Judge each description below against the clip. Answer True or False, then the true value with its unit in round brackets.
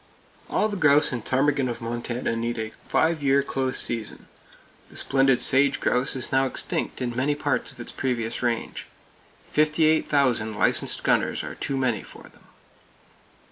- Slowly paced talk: False (165 wpm)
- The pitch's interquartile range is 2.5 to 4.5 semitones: True (3.0 semitones)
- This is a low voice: True (130 Hz)